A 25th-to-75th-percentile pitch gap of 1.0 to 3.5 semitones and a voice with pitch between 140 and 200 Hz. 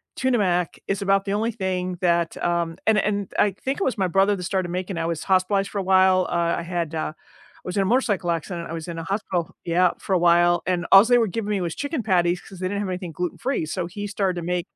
Yes: narrow, 2.6 semitones; medium, 185 Hz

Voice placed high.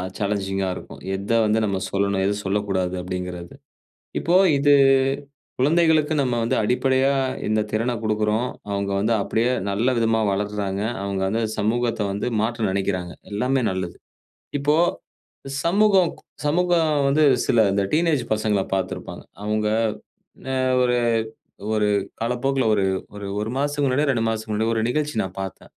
No: low, 110 Hz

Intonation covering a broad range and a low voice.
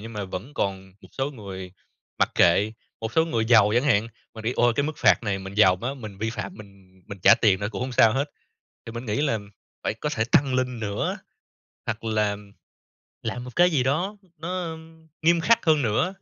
Yes: wide, 5.9 semitones; low, 115 Hz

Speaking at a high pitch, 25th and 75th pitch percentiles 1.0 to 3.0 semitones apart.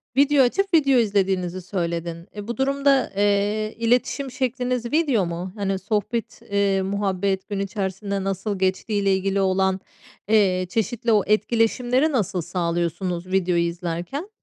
No: high, 200 Hz; average, 4.2 semitones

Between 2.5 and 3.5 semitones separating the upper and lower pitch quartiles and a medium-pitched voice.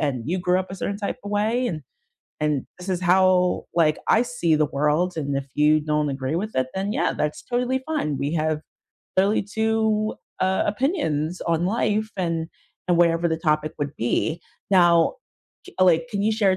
No: average, 5.1 semitones; medium, 180 Hz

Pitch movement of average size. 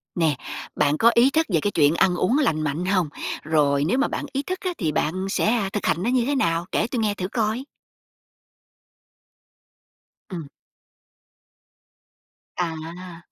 No: wide, 6.4 semitones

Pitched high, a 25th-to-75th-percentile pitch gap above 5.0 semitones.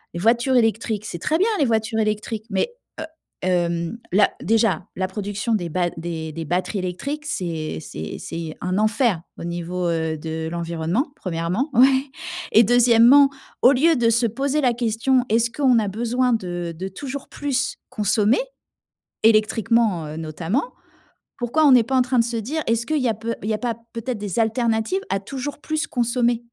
Yes: high, 225 Hz; wide, 5.6 semitones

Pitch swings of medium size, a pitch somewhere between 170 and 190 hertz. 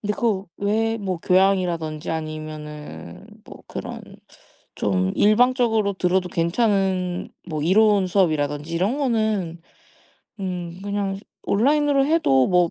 Yes: average, 4.6 semitones; medium, 185 Hz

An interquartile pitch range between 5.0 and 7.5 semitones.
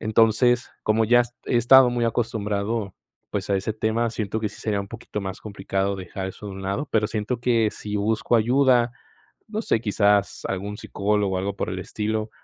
No: average, 2.7 semitones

